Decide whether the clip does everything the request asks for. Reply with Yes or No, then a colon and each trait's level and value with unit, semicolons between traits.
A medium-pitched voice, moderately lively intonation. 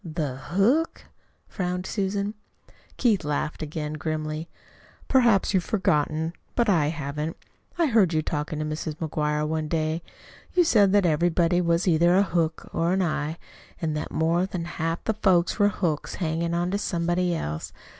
Yes: medium, 170 Hz; average, 3.4 semitones